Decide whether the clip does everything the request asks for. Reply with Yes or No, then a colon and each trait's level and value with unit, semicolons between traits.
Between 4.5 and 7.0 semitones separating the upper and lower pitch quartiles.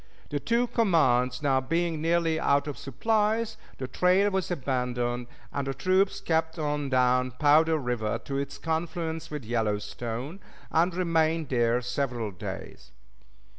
Yes: average, 5.1 semitones